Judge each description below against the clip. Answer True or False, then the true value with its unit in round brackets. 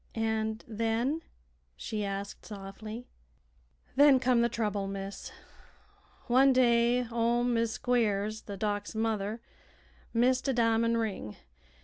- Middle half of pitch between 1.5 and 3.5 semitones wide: True (2.4 semitones)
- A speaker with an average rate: False (110 wpm)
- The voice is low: False (225 Hz)